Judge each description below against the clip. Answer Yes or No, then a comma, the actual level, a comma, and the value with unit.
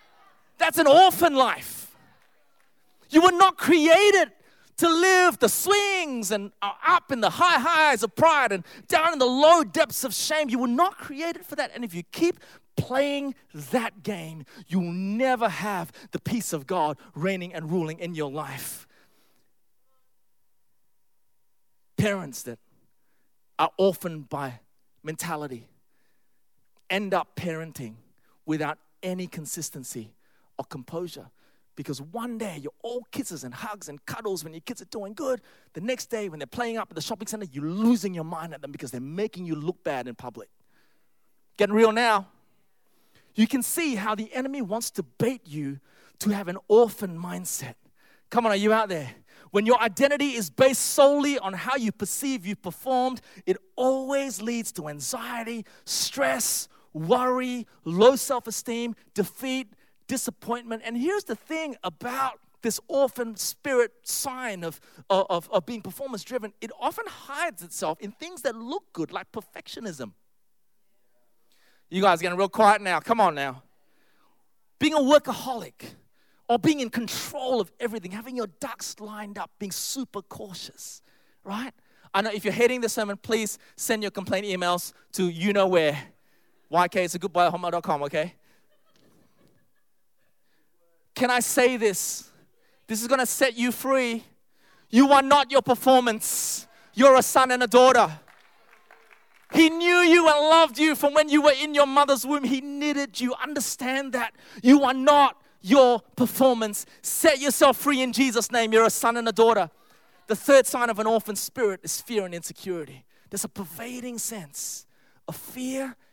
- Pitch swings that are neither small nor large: No, wide, 6.5 semitones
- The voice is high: Yes, high, 225 Hz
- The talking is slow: No, average, 160 wpm